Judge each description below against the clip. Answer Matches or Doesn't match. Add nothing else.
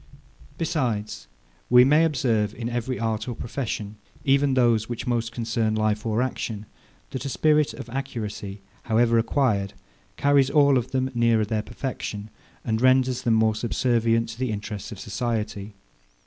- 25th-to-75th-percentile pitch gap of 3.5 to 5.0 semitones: Doesn't match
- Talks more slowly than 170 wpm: Matches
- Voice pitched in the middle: Doesn't match